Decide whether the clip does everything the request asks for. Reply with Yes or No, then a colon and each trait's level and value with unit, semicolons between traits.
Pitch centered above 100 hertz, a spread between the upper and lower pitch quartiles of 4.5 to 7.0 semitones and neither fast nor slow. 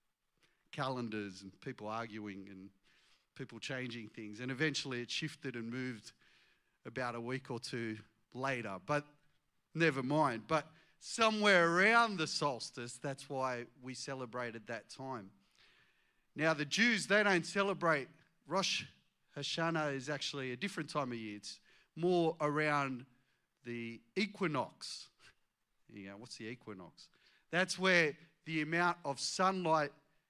No: medium, 140 Hz; average, 5.2 semitones; slow, 125 wpm